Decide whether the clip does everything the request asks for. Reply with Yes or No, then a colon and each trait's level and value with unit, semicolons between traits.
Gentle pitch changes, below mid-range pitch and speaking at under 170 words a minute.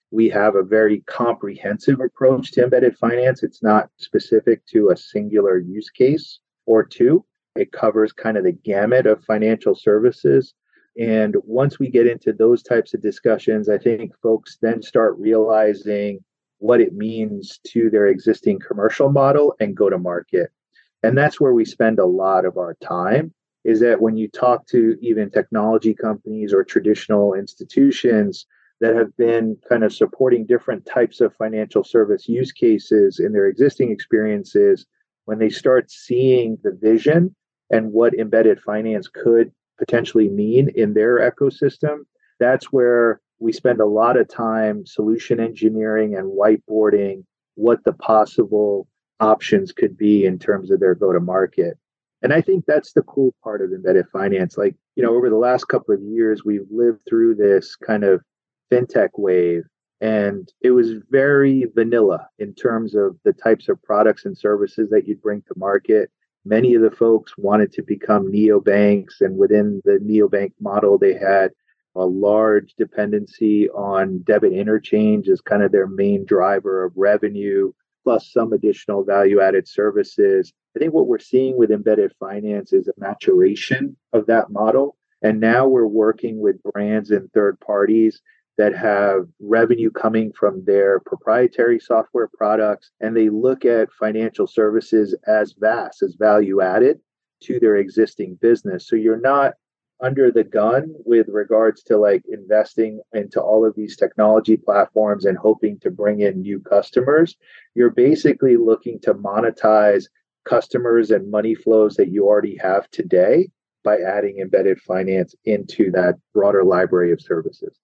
No: average, 4.8 semitones; low, 110 Hz; average, 160 wpm